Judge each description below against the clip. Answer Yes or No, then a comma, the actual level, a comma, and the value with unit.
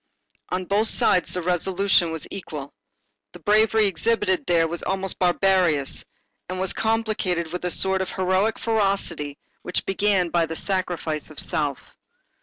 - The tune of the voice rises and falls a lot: No, average, 2.7 semitones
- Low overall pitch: No, medium, 185 Hz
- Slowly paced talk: No, average, 145 wpm